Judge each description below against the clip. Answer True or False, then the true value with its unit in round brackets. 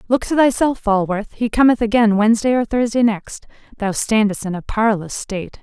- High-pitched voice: True (220 Hz)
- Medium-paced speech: True (180 wpm)